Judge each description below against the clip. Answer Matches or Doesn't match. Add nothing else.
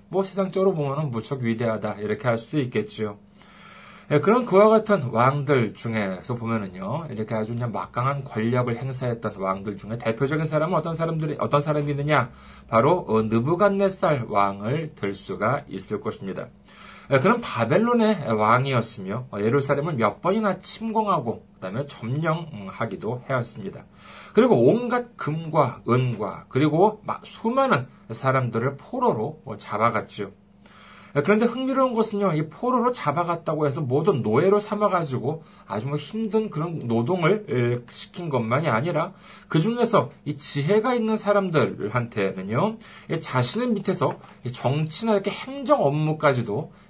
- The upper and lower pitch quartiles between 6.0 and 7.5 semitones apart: Doesn't match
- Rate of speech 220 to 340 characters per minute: Matches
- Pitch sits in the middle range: Matches